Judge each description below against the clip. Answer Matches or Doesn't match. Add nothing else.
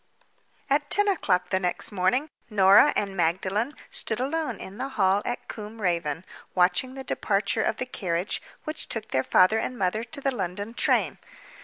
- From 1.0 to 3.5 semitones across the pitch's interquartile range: Doesn't match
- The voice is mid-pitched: Doesn't match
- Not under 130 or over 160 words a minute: Doesn't match